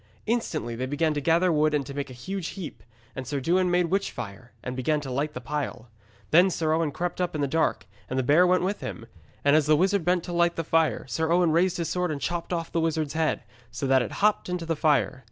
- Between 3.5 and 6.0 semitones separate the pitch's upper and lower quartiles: Yes, average, 3.9 semitones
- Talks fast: Yes, fast, 250 wpm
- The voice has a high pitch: No, medium, 160 Hz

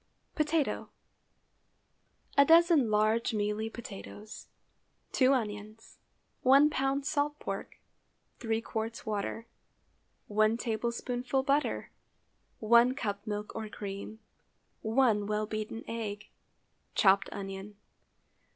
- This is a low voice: No, high, 225 Hz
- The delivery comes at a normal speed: No, slow, 95 wpm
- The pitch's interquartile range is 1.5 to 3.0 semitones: No, average, 3.8 semitones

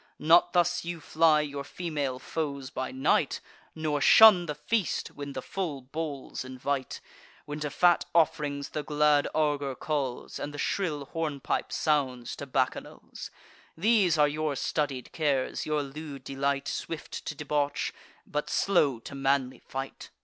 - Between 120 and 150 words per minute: Yes, average, 145 wpm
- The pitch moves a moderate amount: No, narrow, 2.3 semitones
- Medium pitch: Yes, medium, 145 Hz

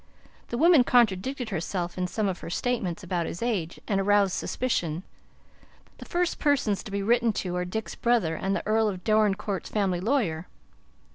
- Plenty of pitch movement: No, average, 4.6 semitones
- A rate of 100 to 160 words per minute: No, average, 170 wpm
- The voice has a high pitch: Yes, high, 200 Hz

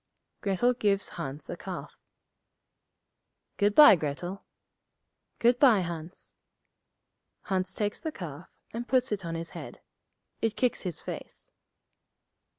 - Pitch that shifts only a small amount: No, wide, 5.5 semitones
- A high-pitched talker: Yes, high, 195 Hz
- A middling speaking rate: No, slow, 120 wpm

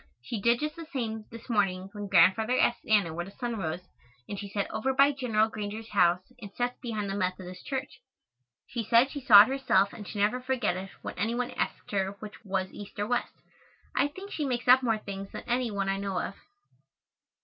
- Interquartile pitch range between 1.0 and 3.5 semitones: No, average, 3.9 semitones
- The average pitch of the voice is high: Yes, high, 215 Hz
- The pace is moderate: No, fast, 215 wpm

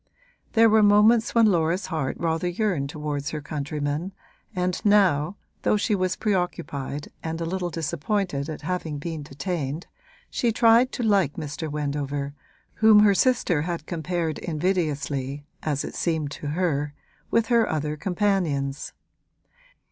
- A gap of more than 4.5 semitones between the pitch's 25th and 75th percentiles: Yes, average, 5.0 semitones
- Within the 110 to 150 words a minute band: Yes, average, 140 wpm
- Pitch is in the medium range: Yes, medium, 165 Hz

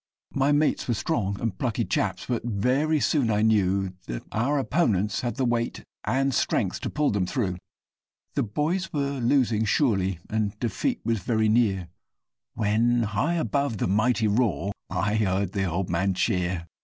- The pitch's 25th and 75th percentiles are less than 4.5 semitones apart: No, average, 4.9 semitones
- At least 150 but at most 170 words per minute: Yes, average, 165 wpm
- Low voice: Yes, low, 110 Hz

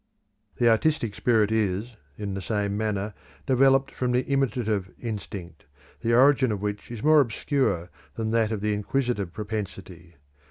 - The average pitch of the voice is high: No, low, 110 Hz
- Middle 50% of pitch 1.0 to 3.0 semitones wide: No, average, 3.4 semitones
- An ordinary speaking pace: Yes, average, 150 wpm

